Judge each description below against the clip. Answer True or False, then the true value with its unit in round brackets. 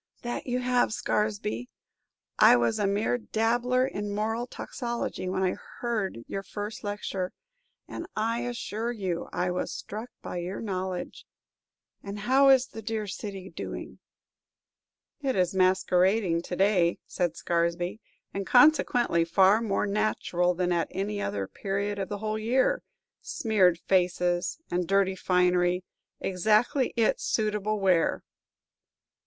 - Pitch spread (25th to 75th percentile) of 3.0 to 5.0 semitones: True (3.6 semitones)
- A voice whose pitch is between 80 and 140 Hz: False (200 Hz)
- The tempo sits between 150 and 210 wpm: False (135 wpm)